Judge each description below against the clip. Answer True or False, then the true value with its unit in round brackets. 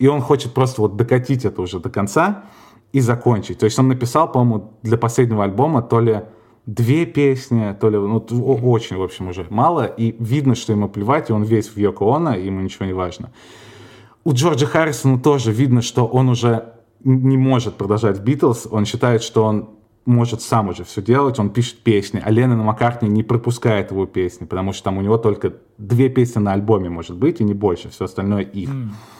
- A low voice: True (115 Hz)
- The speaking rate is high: True (200 wpm)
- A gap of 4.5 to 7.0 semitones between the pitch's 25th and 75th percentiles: False (3.3 semitones)